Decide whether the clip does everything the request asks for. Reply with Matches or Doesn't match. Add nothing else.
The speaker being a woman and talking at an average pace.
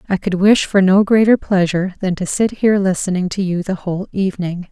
Doesn't match